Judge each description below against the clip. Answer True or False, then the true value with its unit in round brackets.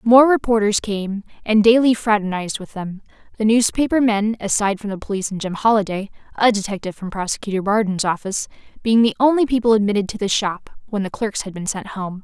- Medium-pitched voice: False (210 Hz)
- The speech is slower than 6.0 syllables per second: False (6.2 syllables/s)